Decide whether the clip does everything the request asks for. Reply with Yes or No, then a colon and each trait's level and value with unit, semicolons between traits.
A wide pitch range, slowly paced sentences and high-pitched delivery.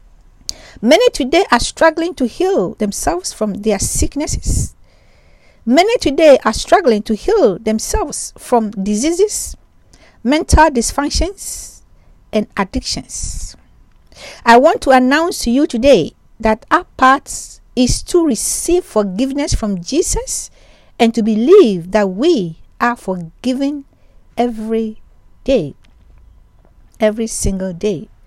Yes: wide, 6.7 semitones; slow, 110 wpm; very high, 250 Hz